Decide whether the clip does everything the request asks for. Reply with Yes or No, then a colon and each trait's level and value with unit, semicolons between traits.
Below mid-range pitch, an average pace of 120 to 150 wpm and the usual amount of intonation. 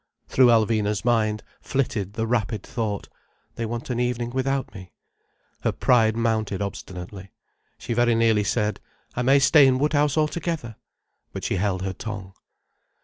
Yes: low, 115 Hz; average, 140 wpm; average, 3.3 semitones